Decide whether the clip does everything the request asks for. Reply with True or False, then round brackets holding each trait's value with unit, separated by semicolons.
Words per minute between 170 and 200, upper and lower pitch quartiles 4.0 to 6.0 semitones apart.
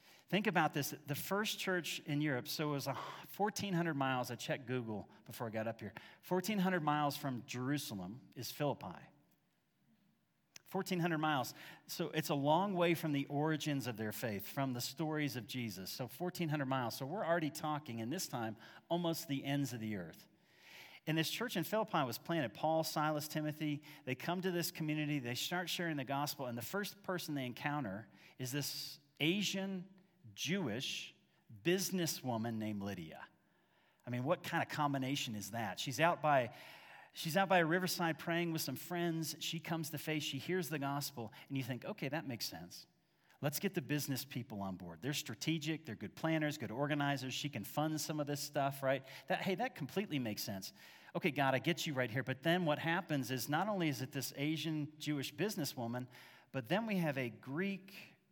True (190 wpm; 4.3 semitones)